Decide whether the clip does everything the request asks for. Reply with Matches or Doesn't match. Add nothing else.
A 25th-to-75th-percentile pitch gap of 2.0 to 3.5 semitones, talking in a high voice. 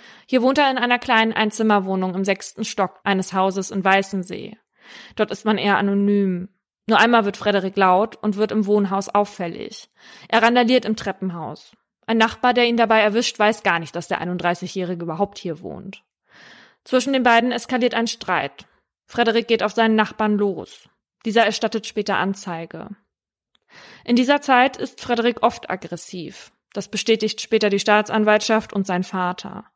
Matches